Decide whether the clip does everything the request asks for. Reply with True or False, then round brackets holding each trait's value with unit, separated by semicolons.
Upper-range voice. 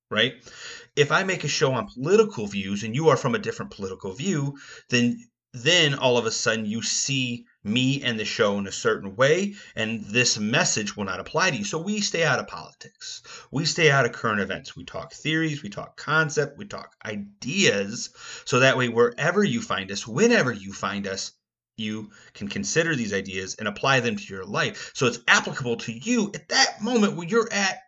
False (140 Hz)